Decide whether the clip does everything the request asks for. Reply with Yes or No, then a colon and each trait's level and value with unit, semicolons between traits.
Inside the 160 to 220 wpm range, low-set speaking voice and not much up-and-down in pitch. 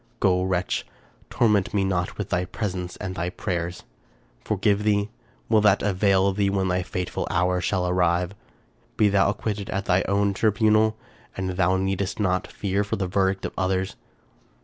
Yes: average, 165 wpm; very low, 95 Hz; narrow, 1.9 semitones